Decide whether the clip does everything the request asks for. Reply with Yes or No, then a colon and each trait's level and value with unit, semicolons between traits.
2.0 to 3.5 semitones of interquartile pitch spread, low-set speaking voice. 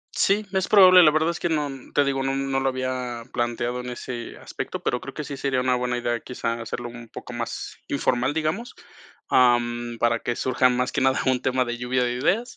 Yes: narrow, 2.4 semitones; low, 130 Hz